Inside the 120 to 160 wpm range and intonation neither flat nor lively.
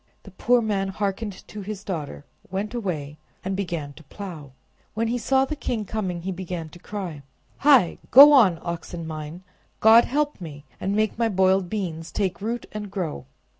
No: average, 175 wpm; average, 4.3 semitones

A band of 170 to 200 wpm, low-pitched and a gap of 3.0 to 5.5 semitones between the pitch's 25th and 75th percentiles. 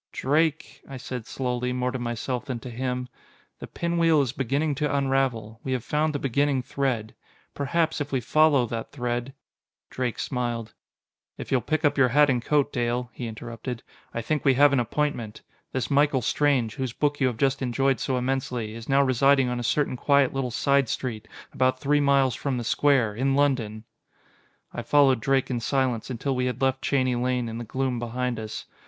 No: average, 190 wpm; low, 130 Hz; narrow, 2.5 semitones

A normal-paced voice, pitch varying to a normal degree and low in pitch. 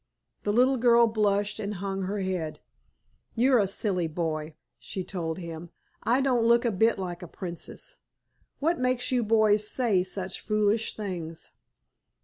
No: average, 150 wpm; average, 4.4 semitones; high, 205 Hz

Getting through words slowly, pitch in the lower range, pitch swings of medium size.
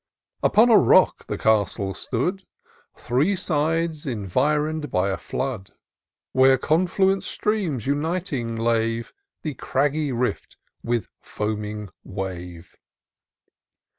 No: slow, 100 wpm; low, 130 Hz; wide, 6.4 semitones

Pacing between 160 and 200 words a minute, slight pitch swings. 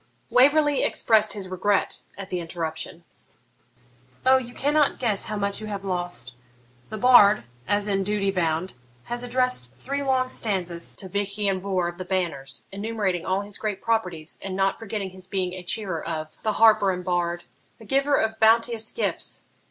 No: average, 170 wpm; average, 3.7 semitones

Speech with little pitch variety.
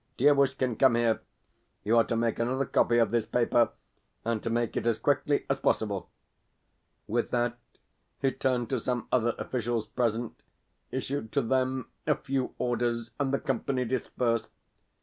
Yes: narrow, 2.1 semitones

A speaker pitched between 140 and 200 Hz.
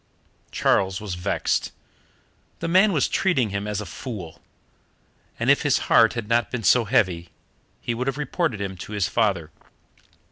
No: low, 110 Hz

